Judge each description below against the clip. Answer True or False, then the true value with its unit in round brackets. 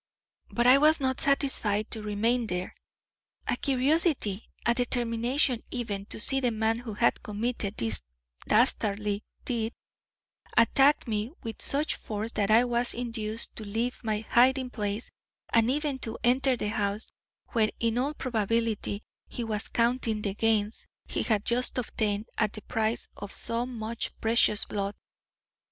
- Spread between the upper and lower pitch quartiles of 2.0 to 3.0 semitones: True (2.7 semitones)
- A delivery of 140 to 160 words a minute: True (150 wpm)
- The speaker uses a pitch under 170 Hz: False (230 Hz)